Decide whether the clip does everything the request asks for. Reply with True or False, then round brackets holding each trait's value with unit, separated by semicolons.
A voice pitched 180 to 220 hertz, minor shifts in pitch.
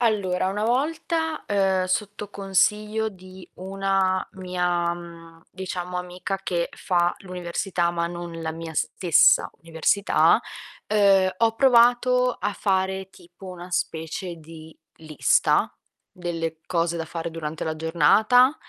False (185 Hz; 3.0 semitones)